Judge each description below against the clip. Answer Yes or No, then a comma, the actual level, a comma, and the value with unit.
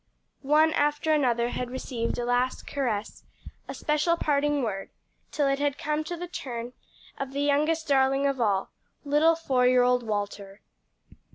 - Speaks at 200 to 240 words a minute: No, average, 160 wpm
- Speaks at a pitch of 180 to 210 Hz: No, very high, 275 Hz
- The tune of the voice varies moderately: Yes, average, 3.4 semitones